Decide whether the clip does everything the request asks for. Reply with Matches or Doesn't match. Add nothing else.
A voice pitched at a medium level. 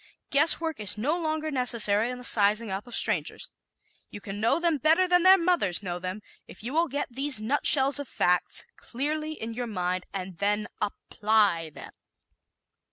Doesn't match